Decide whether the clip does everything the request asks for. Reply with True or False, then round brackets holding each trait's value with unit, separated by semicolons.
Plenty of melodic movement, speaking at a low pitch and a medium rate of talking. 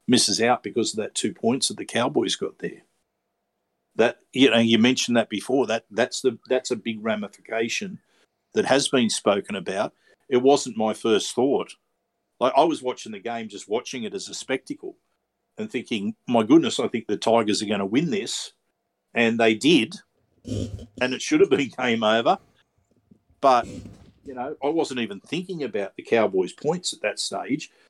True (8.9 semitones; 125 Hz; 185 wpm)